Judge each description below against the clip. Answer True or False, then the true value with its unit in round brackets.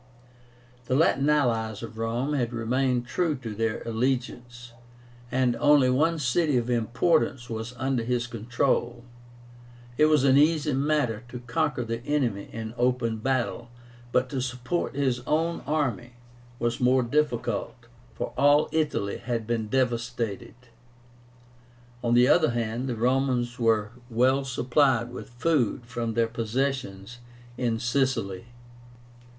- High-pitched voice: False (125 Hz)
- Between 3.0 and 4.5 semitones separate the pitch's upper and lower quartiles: False (2.6 semitones)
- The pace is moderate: False (130 wpm)